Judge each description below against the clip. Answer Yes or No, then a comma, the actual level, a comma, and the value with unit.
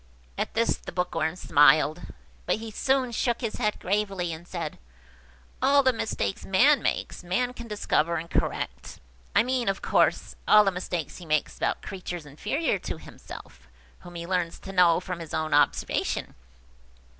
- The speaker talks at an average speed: Yes, average, 155 wpm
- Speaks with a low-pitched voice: No, medium, 180 Hz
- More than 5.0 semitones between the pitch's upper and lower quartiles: Yes, wide, 5.6 semitones